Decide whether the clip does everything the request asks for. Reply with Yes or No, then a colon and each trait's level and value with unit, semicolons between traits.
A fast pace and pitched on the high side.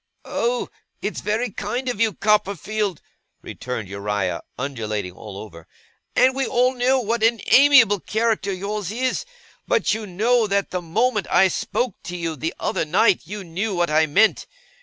No: average, 160 wpm; high, 205 Hz